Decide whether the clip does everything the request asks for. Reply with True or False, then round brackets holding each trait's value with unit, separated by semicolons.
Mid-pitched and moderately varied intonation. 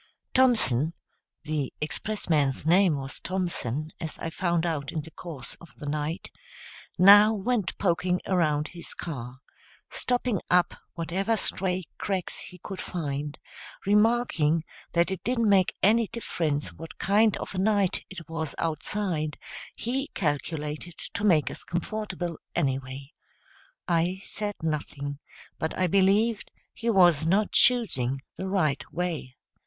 True (175 Hz; 4.7 semitones)